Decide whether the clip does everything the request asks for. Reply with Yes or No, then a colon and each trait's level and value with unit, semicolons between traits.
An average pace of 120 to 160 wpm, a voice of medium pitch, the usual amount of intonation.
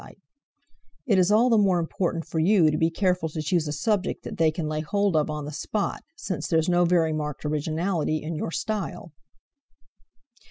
No: average, 190 wpm; medium, 165 Hz; average, 3.6 semitones